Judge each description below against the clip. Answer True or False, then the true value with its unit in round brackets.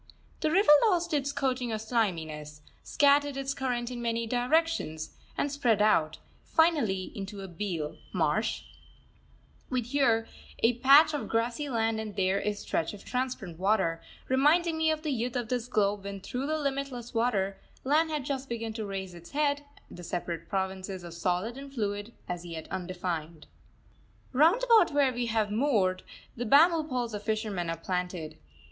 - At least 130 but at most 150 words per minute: False (165 wpm)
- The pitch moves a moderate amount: False (6.5 semitones)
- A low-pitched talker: False (230 Hz)